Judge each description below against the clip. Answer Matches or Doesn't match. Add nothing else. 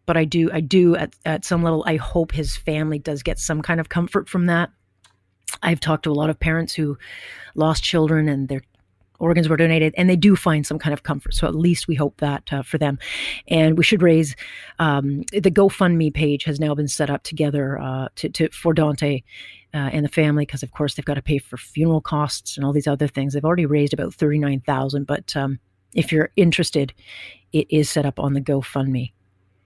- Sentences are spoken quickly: Matches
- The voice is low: Doesn't match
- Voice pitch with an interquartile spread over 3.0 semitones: Doesn't match